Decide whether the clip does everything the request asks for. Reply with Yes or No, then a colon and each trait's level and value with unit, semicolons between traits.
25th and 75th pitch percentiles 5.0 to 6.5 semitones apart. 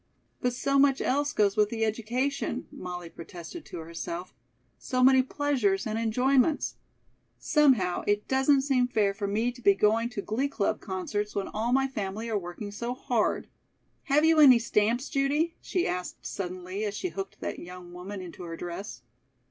Yes: wide, 5.6 semitones